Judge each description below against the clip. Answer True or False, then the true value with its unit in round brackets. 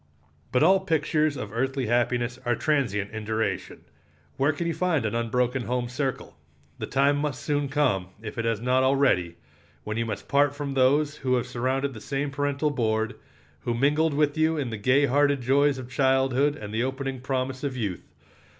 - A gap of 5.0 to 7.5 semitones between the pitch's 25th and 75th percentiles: False (3.2 semitones)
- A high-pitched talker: False (130 Hz)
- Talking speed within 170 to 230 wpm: True (185 wpm)